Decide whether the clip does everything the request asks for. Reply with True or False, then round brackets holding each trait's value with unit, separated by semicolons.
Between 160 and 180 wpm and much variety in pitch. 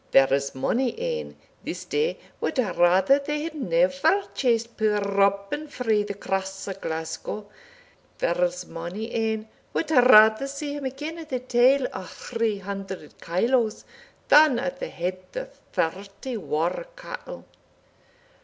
False (135 wpm; 6.4 semitones)